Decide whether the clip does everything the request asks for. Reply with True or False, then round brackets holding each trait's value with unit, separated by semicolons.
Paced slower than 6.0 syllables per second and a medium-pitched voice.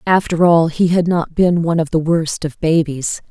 True (4.8 syllables/s; 165 Hz)